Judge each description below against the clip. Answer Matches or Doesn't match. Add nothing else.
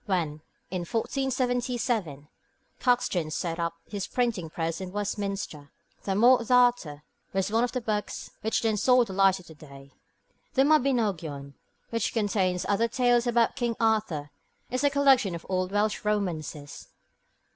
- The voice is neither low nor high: Doesn't match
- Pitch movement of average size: Doesn't match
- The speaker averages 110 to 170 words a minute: Matches